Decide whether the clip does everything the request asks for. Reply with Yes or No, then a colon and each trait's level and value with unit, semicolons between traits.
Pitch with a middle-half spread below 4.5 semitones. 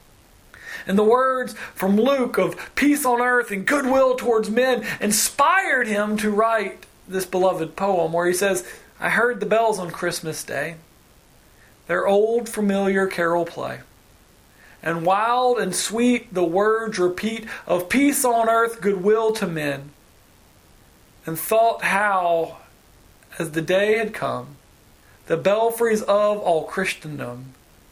No: average, 5.2 semitones